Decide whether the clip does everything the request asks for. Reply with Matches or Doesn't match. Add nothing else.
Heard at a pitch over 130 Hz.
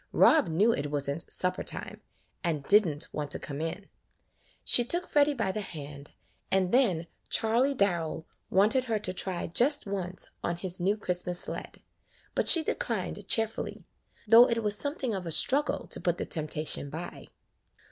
Matches